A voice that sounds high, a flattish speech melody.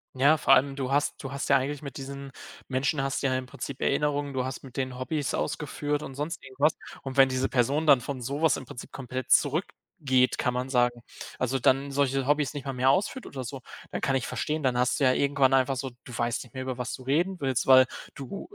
No: low, 135 Hz; narrow, 1.7 semitones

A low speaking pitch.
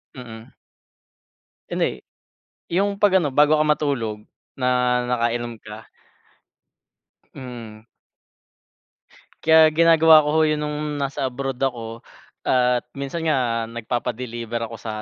Yes: low, 130 Hz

